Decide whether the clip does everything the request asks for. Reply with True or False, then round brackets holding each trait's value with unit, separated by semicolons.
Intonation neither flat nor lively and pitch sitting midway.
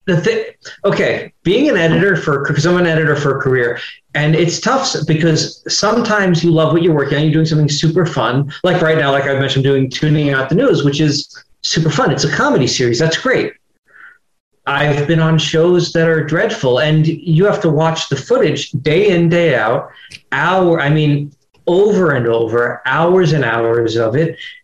True (3.4 semitones; 155 Hz)